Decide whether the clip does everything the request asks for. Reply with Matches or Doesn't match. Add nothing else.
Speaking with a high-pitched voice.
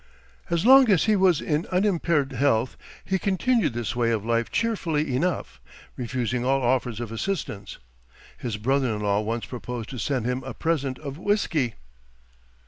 Doesn't match